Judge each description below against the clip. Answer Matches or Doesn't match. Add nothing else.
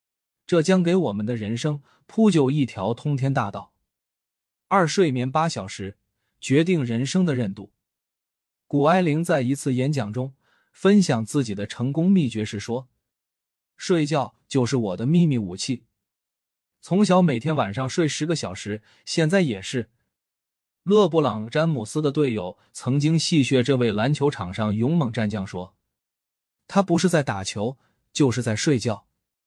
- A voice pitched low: Matches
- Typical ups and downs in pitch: Doesn't match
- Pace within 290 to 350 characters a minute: Doesn't match